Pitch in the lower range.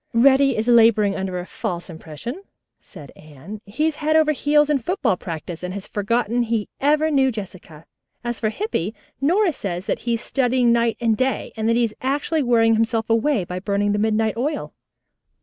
No: high, 230 Hz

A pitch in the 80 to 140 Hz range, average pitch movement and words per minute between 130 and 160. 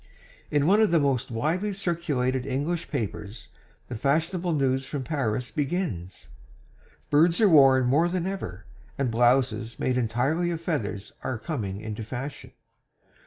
No: low, 135 Hz; wide, 5.7 semitones; average, 140 wpm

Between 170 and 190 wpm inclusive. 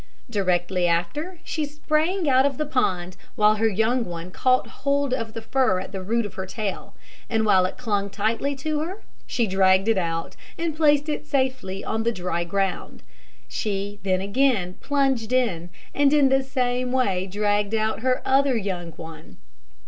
Yes: average, 175 wpm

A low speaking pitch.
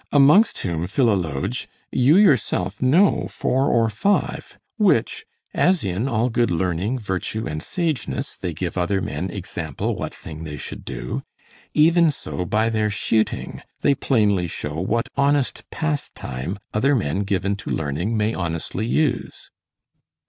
Yes: low, 110 Hz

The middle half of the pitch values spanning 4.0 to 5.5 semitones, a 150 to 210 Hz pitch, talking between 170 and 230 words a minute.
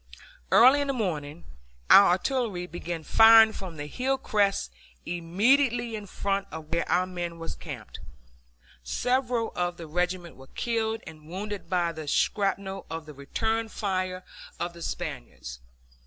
No: average, 5.0 semitones; medium, 185 Hz; average, 145 wpm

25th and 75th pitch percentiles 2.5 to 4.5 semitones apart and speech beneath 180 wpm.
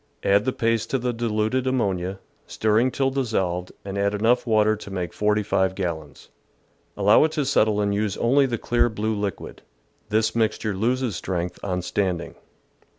Yes: average, 3.5 semitones; average, 160 wpm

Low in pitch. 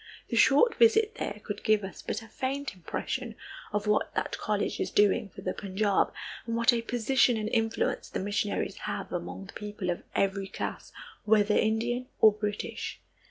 No: high, 215 Hz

